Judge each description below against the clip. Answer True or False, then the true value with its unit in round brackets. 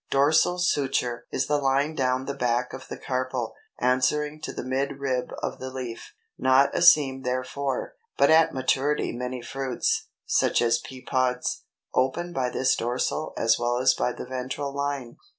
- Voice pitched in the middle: False (130 Hz)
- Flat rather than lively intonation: True (1.8 semitones)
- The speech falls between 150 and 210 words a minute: True (165 wpm)